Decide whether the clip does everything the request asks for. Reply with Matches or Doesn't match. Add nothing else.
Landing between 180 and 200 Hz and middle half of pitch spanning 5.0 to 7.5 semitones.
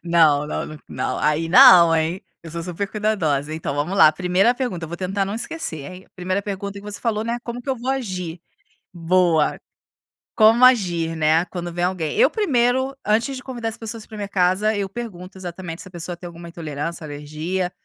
Doesn't match